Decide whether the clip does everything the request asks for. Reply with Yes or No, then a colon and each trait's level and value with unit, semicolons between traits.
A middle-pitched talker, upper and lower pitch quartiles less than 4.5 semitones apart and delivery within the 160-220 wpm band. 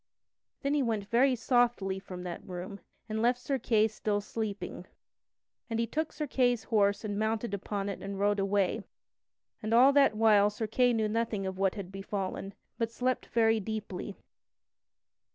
No: high, 215 Hz; average, 2.8 semitones; average, 165 wpm